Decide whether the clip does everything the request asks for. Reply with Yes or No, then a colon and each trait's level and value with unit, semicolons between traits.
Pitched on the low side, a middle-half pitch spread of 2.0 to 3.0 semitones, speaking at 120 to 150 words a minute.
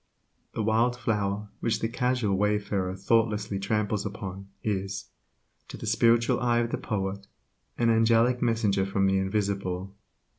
Yes: low, 105 Hz; average, 2.7 semitones; average, 140 wpm